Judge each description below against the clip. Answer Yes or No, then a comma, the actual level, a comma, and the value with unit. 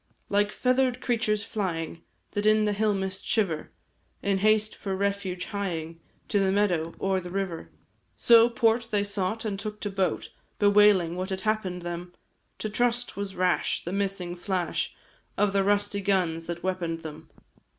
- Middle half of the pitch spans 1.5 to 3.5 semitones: Yes, average, 2.7 semitones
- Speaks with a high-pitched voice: Yes, high, 195 Hz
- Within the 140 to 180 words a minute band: Yes, average, 160 wpm